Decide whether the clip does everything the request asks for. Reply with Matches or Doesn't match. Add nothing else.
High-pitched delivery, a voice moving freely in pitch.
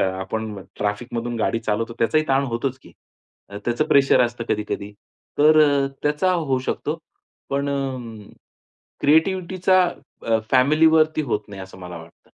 Doesn't match